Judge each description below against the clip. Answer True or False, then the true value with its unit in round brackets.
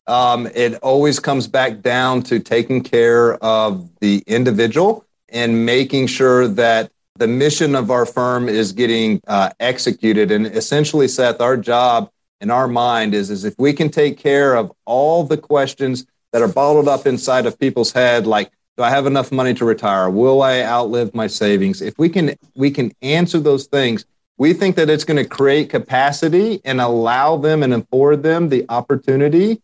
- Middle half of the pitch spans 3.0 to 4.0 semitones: True (3.4 semitones)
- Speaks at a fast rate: False (180 wpm)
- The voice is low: True (130 Hz)